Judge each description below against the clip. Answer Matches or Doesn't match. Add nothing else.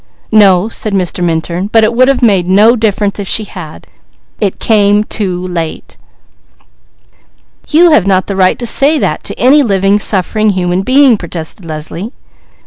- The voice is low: Doesn't match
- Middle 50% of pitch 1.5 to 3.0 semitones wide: Doesn't match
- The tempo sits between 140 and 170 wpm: Matches